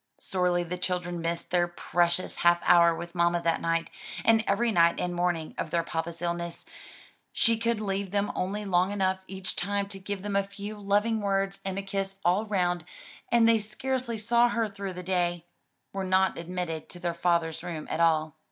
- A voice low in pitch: No, medium, 185 Hz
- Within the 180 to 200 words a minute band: Yes, average, 190 wpm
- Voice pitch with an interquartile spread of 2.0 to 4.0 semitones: Yes, average, 2.8 semitones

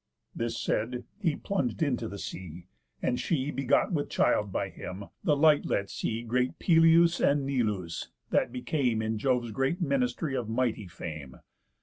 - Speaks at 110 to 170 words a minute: Yes, average, 155 wpm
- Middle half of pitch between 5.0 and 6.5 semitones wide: Yes, wide, 5.4 semitones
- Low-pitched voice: Yes, low, 125 Hz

